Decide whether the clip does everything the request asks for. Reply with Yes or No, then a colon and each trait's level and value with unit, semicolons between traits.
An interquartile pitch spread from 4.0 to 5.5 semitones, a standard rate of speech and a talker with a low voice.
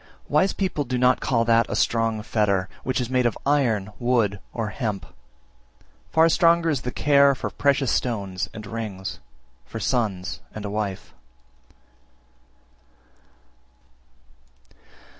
No: average, 4.4 semitones; slow, 130 wpm; low, 115 Hz